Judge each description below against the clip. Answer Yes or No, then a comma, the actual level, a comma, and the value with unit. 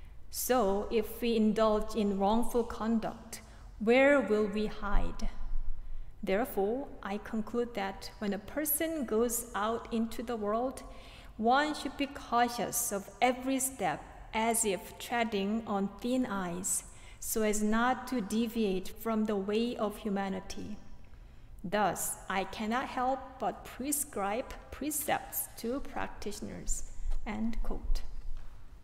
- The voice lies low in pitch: No, high, 225 Hz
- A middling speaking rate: No, slow, 120 wpm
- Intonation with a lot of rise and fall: No, average, 3.3 semitones